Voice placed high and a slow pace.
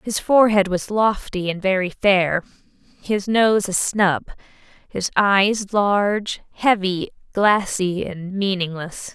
Yes: high, 195 Hz; slow, 120 wpm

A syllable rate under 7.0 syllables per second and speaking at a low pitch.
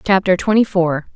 No: 5.2 syllables/s; medium, 185 Hz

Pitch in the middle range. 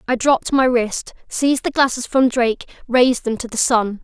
No: high, 245 Hz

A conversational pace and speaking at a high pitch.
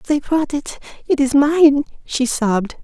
Yes: average, 170 wpm; very high, 280 Hz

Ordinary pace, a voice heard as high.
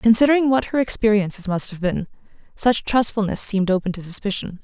Yes: average, 170 wpm; high, 210 Hz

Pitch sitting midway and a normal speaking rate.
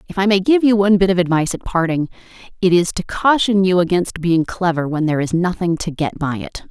No: medium, 180 Hz; fast, 240 wpm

